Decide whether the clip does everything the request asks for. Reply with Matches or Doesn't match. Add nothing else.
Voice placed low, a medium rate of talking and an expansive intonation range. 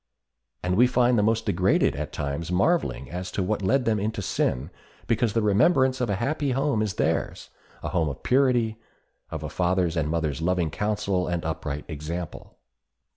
Matches